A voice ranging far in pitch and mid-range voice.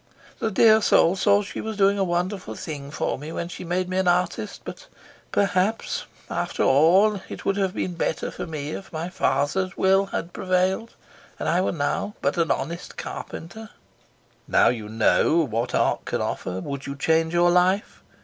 No: average, 3.7 semitones; medium, 180 Hz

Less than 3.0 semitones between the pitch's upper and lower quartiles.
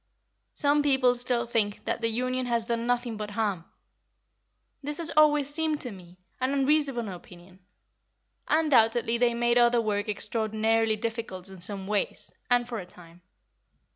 No: average, 3.4 semitones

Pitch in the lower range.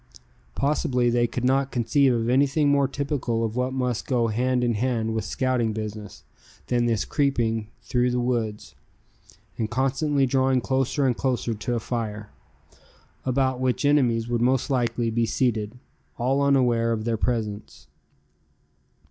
Yes: low, 125 Hz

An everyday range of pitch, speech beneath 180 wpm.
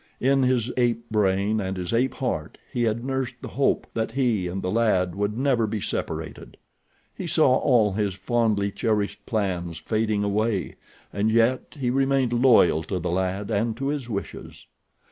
Yes: average, 3.9 semitones; average, 170 wpm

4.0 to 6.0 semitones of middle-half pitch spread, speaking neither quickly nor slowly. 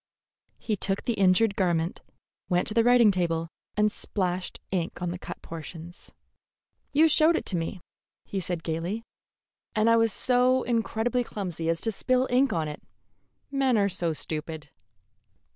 Yes: average, 5.3 semitones; average, 160 wpm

